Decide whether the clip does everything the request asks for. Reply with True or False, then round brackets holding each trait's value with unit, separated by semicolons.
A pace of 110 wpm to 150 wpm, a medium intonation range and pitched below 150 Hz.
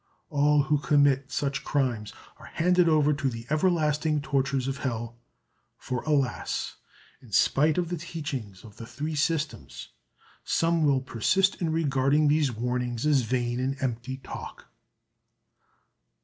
True (135 wpm; 3.5 semitones; 140 Hz)